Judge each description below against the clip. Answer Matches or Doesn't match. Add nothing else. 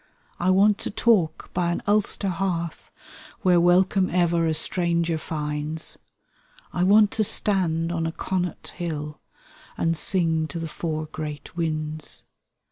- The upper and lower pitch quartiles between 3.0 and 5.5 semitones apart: Doesn't match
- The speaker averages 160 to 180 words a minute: Doesn't match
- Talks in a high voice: Doesn't match